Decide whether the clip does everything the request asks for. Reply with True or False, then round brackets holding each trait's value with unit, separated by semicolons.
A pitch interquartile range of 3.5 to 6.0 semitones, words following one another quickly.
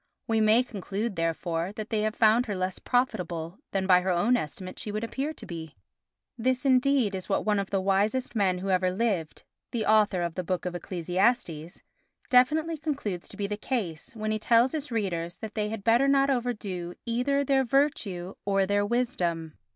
False (5.1 semitones; 185 wpm)